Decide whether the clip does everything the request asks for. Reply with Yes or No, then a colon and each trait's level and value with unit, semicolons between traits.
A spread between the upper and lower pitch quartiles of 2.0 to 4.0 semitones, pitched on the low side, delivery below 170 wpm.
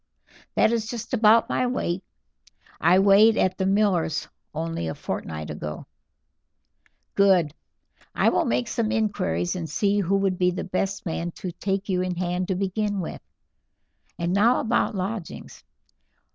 No: average, 3.3 semitones; high, 190 Hz; average, 150 wpm